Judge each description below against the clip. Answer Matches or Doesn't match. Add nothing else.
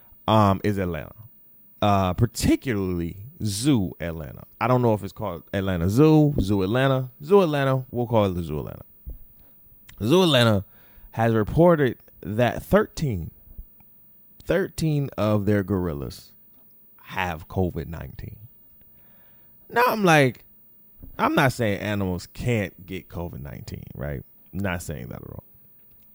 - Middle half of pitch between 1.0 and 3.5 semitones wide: Doesn't match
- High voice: Doesn't match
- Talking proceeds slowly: Matches